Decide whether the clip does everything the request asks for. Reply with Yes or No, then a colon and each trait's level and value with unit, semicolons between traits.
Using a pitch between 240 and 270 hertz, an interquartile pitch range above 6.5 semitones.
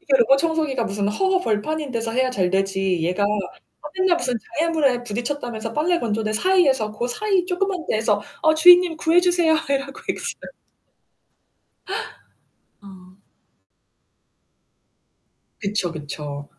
Yes: very high, 250 Hz; wide, 7.8 semitones